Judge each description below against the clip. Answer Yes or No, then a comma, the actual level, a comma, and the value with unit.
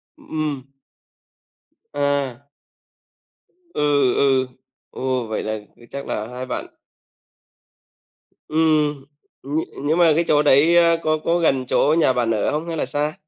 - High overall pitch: No, medium, 145 Hz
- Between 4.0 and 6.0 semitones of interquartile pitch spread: No, average, 3.2 semitones